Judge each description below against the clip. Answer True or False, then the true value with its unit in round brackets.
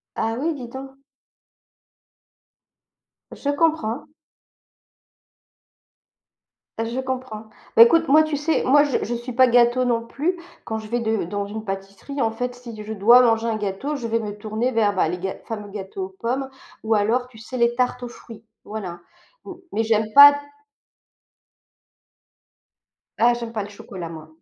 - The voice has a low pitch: False (230 Hz)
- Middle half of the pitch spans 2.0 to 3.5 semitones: True (3.1 semitones)